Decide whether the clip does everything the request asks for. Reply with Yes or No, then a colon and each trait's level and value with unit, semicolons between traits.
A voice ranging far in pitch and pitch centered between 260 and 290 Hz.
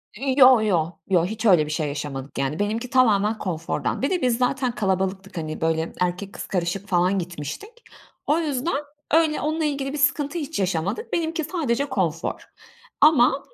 No: wide, 8.2 semitones; high, 215 Hz